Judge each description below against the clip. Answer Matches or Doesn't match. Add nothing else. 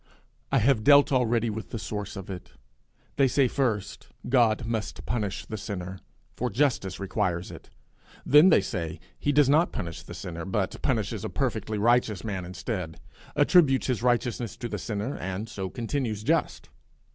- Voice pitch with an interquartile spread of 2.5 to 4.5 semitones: Doesn't match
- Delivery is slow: Doesn't match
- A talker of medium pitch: Doesn't match